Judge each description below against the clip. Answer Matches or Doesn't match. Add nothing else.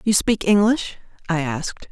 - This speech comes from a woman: Matches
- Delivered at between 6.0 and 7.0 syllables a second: Doesn't match